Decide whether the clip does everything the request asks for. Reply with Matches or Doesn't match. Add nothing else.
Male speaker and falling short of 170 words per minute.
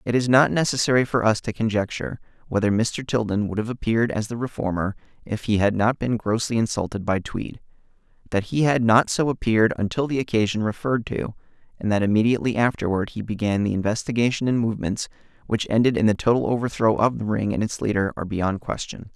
Doesn't match